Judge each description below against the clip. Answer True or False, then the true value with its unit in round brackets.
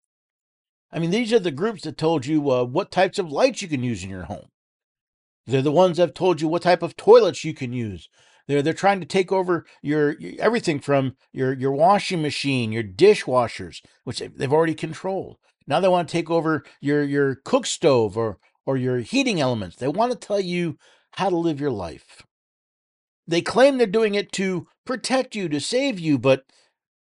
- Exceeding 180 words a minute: True (200 wpm)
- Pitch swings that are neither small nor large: False (6.0 semitones)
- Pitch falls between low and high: True (165 Hz)